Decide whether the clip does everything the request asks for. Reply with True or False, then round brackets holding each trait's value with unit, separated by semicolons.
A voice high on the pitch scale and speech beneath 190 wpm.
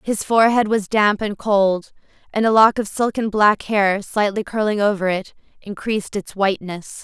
True (205 Hz; 170 wpm)